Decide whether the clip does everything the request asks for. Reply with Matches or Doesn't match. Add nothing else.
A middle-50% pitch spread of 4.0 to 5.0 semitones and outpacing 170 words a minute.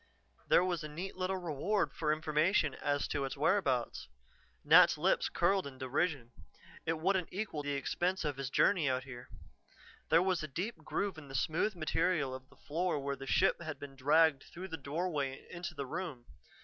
Matches